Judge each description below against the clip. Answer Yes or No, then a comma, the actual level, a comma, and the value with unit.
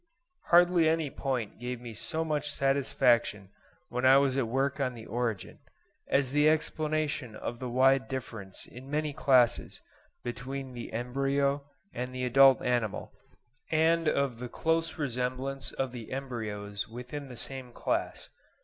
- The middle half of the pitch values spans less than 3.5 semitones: Yes, narrow, 2.6 semitones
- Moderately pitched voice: No, low, 130 Hz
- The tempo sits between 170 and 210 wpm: No, average, 145 wpm